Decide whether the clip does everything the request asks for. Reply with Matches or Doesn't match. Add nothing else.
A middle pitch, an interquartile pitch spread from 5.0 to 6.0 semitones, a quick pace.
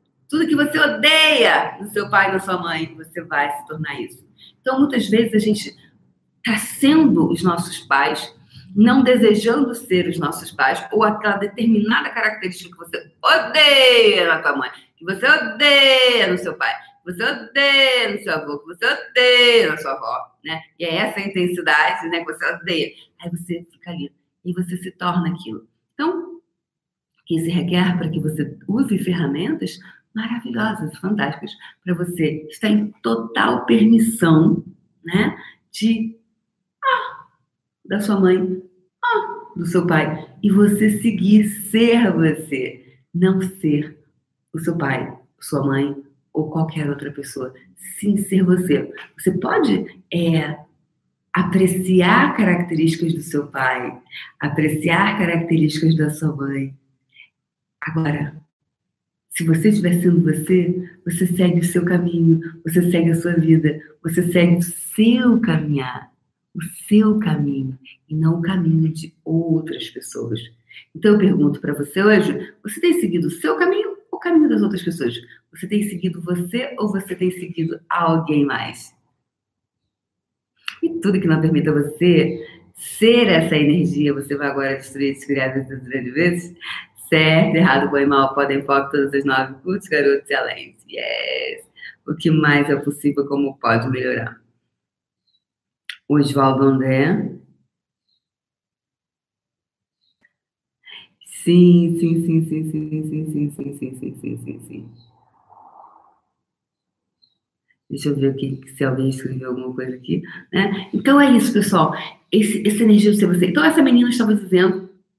Doesn't match